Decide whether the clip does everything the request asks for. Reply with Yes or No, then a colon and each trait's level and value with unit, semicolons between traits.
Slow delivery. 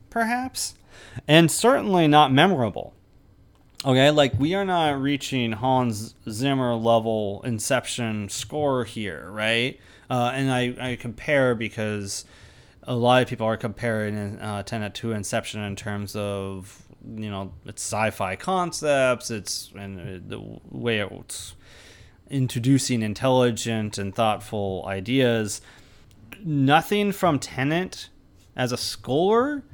Yes: slow, 115 wpm